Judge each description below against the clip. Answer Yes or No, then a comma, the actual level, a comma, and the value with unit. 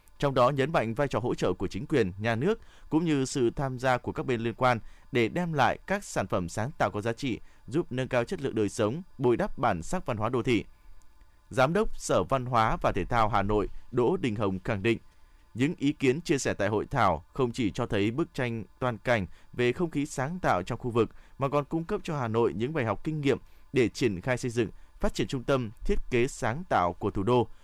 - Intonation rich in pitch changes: No, average, 4.7 semitones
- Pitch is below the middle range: Yes, low, 125 Hz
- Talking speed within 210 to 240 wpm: No, fast, 250 wpm